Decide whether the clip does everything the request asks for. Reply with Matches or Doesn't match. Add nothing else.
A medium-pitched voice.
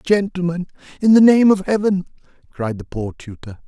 Matches